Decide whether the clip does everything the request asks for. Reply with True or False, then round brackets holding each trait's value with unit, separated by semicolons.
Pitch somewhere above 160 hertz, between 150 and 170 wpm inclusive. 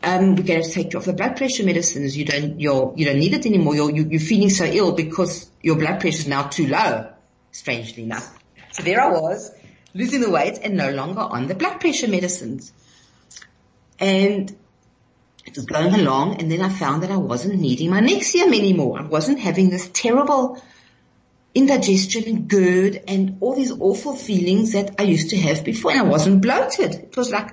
False (190 Hz; 200 wpm)